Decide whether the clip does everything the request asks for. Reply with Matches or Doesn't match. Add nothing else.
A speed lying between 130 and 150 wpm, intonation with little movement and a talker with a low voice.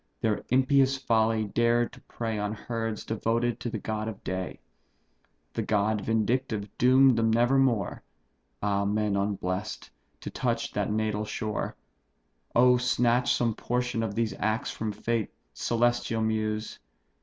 Matches